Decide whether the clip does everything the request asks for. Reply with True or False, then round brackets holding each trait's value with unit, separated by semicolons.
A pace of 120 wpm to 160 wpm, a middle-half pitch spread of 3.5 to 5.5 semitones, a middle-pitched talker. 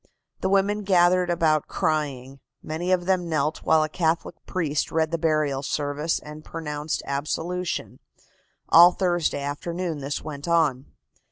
False (140 wpm; 3.0 semitones; 160 Hz)